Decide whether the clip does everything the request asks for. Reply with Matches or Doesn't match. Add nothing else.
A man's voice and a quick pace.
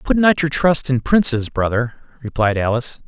Doesn't match